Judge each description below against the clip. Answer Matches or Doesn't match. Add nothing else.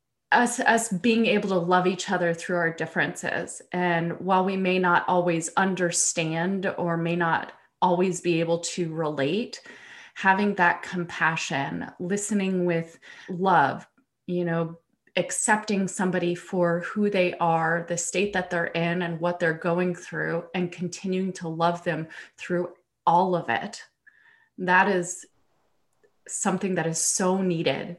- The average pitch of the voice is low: Doesn't match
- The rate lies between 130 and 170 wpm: Matches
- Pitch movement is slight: Matches